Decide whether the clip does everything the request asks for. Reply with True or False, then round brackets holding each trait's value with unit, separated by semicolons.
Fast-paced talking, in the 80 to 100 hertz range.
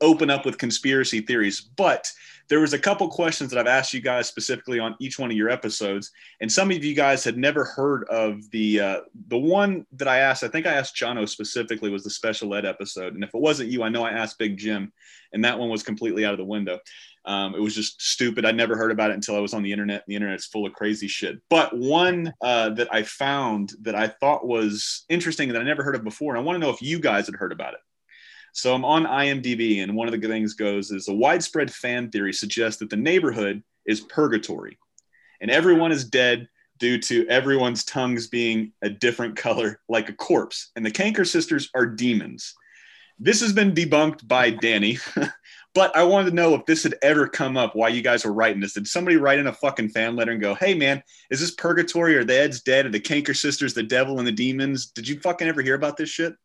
False (240 wpm; 120 Hz)